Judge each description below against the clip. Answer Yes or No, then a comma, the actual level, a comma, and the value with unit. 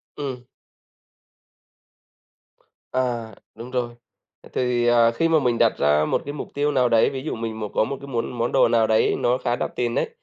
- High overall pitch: No, low, 120 Hz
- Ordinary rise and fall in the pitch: No, narrow, 2.1 semitones